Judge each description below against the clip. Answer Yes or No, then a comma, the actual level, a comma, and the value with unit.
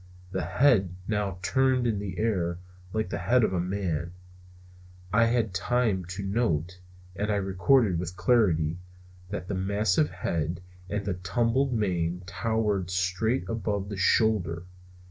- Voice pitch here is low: Yes, very low, 95 Hz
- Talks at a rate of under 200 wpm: Yes, average, 145 wpm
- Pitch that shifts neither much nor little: Yes, average, 3.7 semitones